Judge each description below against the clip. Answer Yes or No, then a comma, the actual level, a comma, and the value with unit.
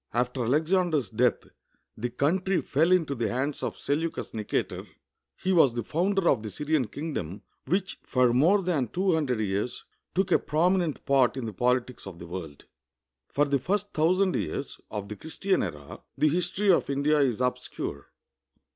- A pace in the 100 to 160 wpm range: No, average, 170 wpm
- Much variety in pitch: Yes, wide, 6.4 semitones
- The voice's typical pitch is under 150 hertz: Yes, medium, 140 Hz